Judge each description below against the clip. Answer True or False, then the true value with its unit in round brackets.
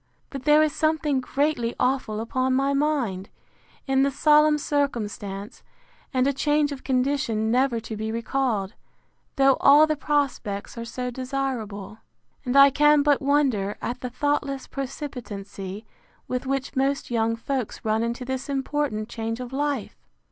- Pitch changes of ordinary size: True (3.7 semitones)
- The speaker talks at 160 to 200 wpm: False (150 wpm)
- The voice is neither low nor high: False (260 Hz)